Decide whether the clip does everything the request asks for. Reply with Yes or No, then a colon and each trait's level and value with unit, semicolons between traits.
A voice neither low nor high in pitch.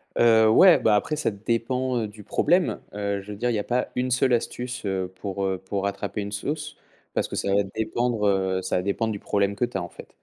No: low, 105 Hz